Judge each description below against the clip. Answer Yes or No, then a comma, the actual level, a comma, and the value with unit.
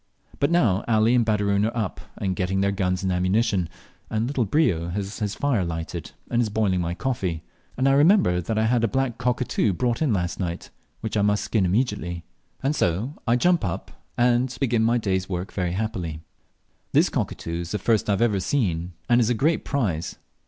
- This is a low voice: Yes, low, 105 Hz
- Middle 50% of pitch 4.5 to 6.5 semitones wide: Yes, average, 4.8 semitones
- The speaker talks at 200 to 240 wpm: Yes, fast, 205 wpm